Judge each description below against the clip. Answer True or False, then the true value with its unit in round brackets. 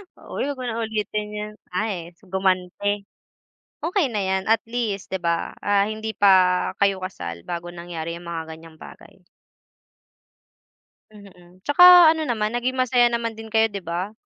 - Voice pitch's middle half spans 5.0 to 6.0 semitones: False (4.1 semitones)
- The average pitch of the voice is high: True (205 Hz)